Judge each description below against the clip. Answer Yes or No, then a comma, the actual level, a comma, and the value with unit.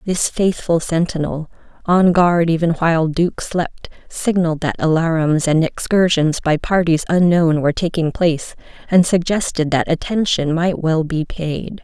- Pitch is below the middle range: No, medium, 165 Hz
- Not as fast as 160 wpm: Yes, average, 140 wpm